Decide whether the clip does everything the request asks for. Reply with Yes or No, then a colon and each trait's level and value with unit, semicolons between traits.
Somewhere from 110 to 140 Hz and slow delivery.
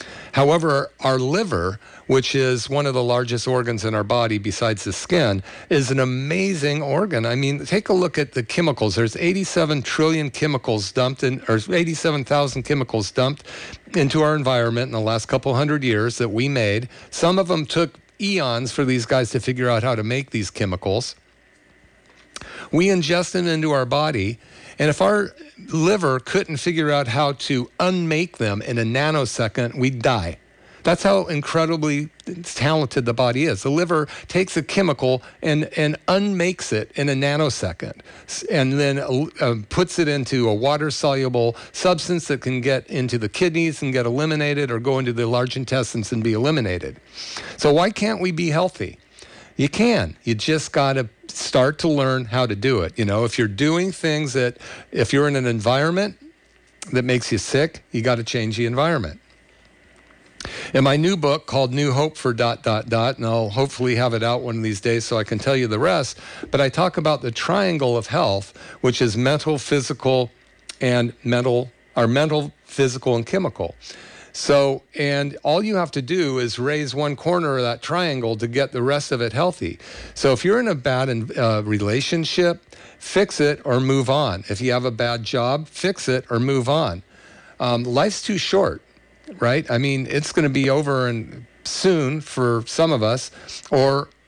No: low, 135 Hz; average, 180 wpm